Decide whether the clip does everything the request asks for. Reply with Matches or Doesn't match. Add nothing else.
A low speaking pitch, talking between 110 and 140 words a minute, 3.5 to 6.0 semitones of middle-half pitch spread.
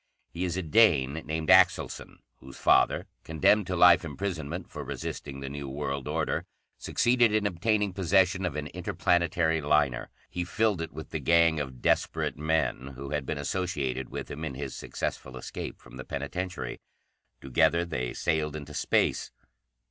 Doesn't match